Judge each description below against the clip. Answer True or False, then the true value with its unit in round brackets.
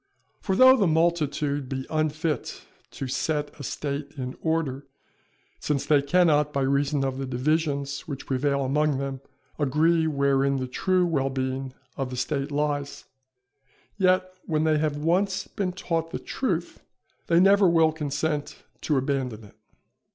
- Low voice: False (145 Hz)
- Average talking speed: True (150 wpm)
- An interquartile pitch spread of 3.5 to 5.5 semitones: False (3.0 semitones)